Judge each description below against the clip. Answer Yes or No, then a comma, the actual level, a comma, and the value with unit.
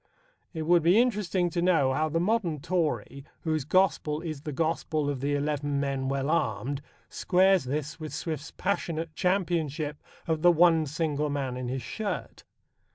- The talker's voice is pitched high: No, medium, 155 Hz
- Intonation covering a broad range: No, average, 3.5 semitones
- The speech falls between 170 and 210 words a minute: No, average, 160 wpm